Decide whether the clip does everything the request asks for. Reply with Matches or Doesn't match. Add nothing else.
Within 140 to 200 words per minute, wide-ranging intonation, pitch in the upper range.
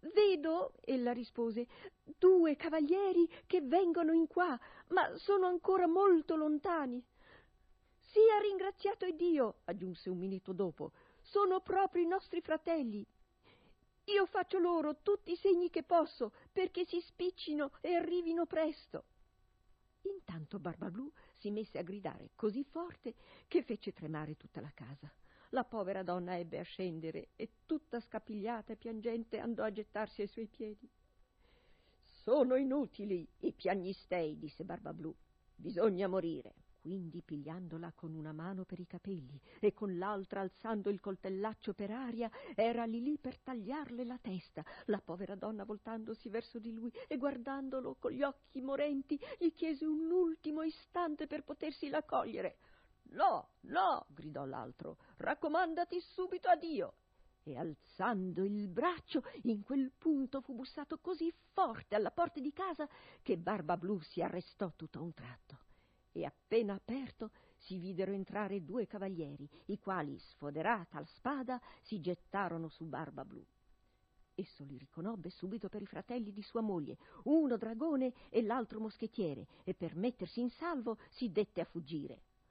Matches